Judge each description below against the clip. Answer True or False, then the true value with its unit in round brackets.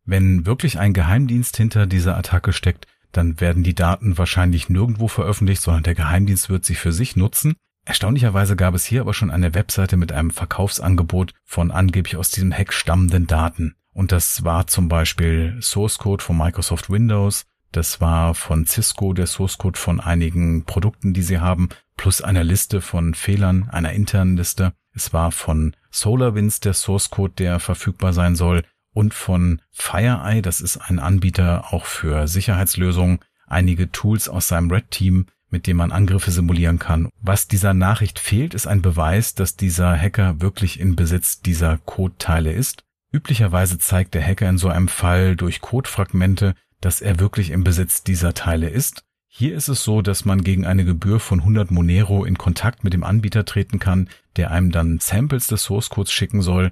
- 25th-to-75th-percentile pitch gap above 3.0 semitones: False (2.6 semitones)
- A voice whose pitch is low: True (95 Hz)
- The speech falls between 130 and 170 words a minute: False (180 wpm)